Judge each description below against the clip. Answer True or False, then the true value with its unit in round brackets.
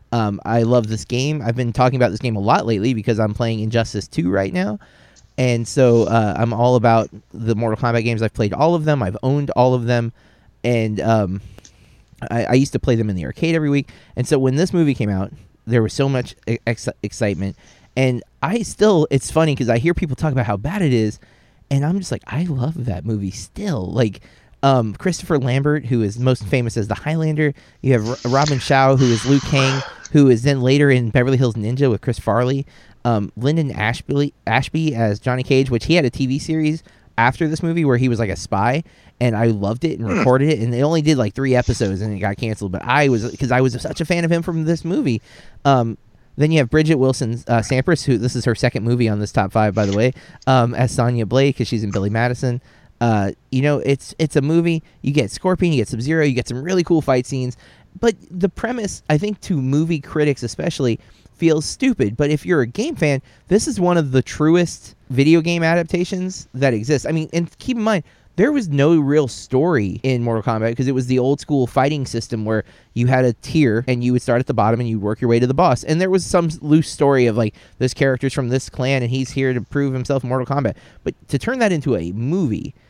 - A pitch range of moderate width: True (4.4 semitones)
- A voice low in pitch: True (130 Hz)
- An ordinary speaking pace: False (235 wpm)